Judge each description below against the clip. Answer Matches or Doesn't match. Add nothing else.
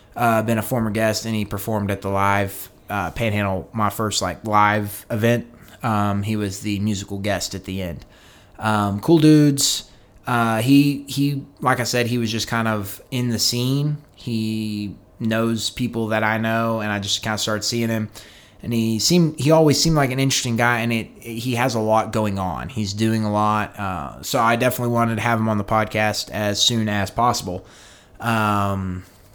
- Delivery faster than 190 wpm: Matches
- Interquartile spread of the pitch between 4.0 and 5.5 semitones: Doesn't match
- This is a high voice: Doesn't match